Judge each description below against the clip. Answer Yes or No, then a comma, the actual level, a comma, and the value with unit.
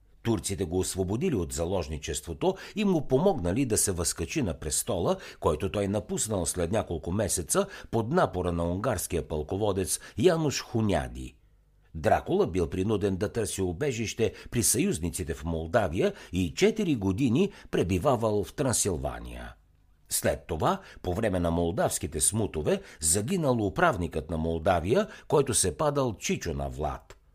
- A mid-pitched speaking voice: No, very low, 95 Hz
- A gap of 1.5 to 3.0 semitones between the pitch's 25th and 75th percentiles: No, average, 4.6 semitones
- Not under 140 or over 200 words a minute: No, average, 130 wpm